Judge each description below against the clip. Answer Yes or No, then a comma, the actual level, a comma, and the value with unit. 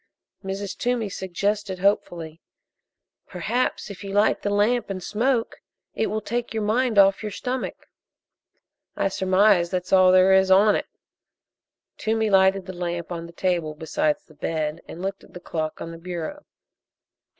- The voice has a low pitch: No, high, 195 Hz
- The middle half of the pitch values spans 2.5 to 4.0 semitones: Yes, average, 3.3 semitones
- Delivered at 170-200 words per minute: No, average, 160 wpm